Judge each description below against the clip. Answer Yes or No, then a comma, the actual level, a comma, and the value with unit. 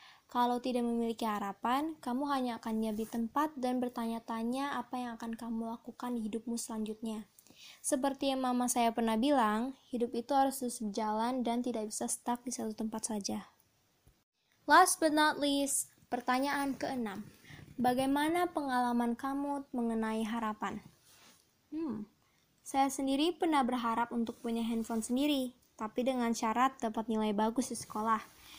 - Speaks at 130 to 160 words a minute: Yes, fast, 140 wpm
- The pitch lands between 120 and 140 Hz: No, high, 240 Hz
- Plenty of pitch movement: No, average, 3.0 semitones